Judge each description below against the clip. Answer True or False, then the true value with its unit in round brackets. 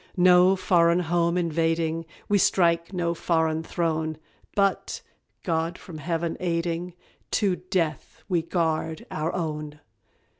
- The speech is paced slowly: True (115 wpm)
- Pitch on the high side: False (170 Hz)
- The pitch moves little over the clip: True (1.8 semitones)